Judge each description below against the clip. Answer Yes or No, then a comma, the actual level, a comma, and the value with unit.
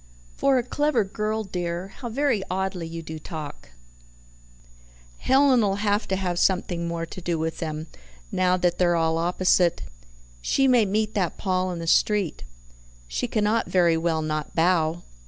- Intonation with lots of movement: No, average, 4.1 semitones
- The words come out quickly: No, average, 155 wpm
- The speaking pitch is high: No, medium, 180 Hz